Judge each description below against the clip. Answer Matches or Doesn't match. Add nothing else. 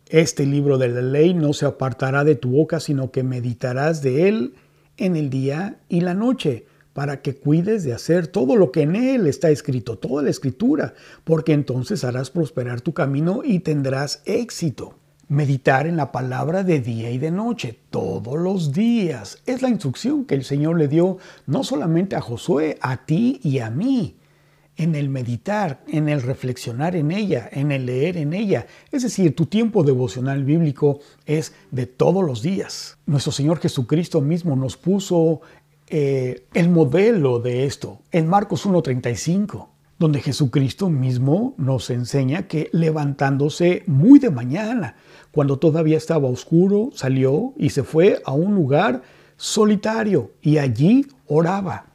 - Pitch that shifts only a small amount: Doesn't match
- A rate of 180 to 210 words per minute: Doesn't match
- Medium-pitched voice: Matches